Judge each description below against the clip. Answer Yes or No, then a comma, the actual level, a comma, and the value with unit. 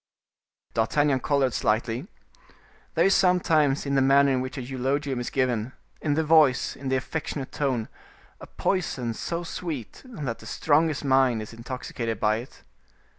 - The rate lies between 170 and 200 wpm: No, average, 155 wpm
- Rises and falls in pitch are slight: No, average, 3.3 semitones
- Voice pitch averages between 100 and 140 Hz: Yes, low, 135 Hz